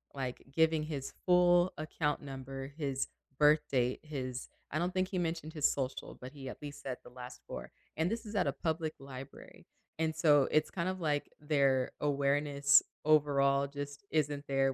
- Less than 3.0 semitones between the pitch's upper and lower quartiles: Yes, narrow, 2.6 semitones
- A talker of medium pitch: Yes, medium, 145 Hz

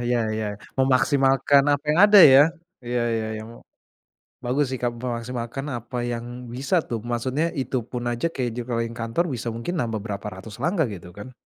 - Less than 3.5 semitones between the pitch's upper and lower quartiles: Yes, narrow, 2.5 semitones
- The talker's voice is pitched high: No, low, 120 Hz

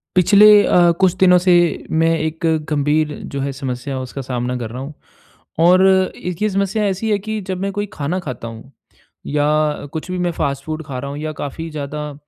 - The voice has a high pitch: No, medium, 155 Hz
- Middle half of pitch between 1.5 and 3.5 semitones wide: No, average, 4.5 semitones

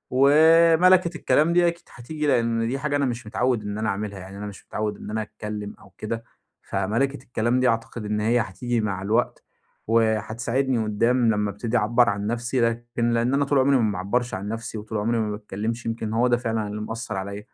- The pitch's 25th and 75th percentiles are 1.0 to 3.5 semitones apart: Yes, average, 3.0 semitones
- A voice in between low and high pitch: No, low, 115 Hz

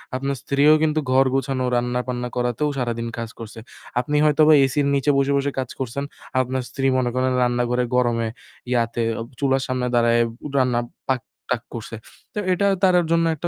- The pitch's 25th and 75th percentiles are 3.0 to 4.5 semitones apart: No, narrow, 2.4 semitones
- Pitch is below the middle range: Yes, low, 130 Hz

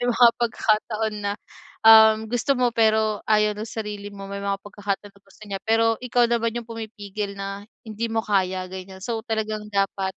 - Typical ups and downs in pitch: No, narrow, 2.1 semitones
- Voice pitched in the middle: No, high, 215 Hz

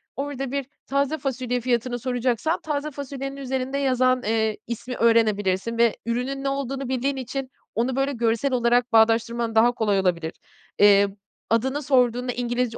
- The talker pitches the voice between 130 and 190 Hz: No, high, 245 Hz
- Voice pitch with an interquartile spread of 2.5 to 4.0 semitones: Yes, average, 2.8 semitones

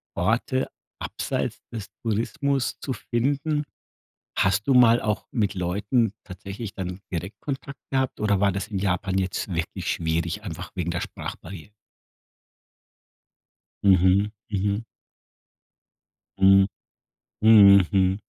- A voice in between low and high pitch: No, low, 100 Hz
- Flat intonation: No, average, 3.5 semitones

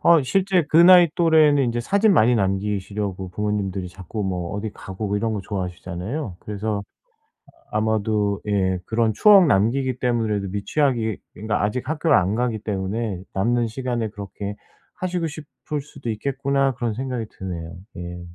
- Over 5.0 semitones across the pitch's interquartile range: Yes, wide, 5.4 semitones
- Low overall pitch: Yes, low, 110 Hz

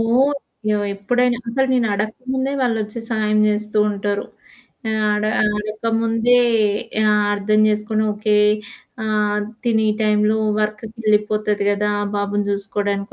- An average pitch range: No, narrow, 1.4 semitones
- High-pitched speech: Yes, high, 215 Hz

